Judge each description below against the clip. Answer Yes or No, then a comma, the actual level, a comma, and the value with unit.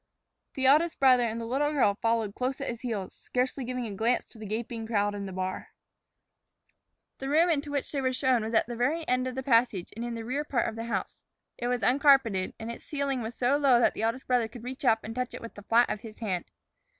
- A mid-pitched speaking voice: No, high, 240 Hz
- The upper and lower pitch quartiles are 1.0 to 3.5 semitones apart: Yes, average, 2.8 semitones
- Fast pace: Yes, fast, 250 wpm